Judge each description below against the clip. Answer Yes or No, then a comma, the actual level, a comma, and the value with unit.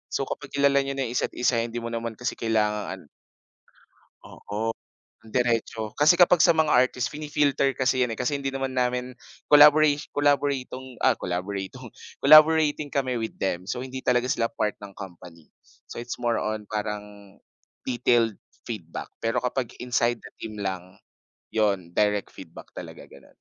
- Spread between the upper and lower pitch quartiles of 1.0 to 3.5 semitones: No, average, 4.2 semitones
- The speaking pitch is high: No, low, 120 Hz